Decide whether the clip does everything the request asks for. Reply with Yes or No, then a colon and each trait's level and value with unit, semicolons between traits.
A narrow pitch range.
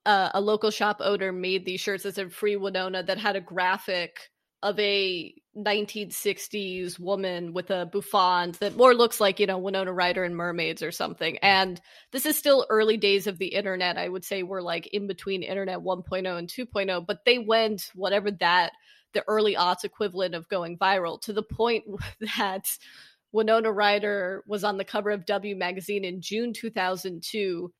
Yes: narrow, 2.2 semitones